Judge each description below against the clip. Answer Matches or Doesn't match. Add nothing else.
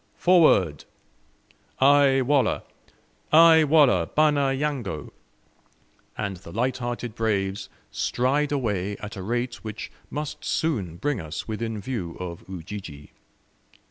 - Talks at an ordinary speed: Doesn't match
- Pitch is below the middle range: Matches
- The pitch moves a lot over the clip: Matches